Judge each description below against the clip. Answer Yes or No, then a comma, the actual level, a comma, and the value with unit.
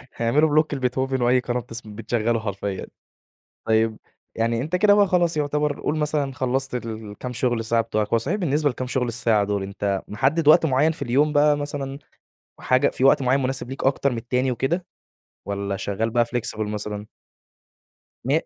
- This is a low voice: Yes, low, 125 Hz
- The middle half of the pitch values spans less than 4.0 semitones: No, average, 4.3 semitones